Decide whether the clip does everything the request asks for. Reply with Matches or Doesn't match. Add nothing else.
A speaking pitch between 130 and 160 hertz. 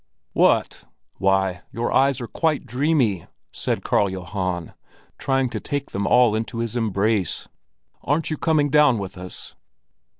Doesn't match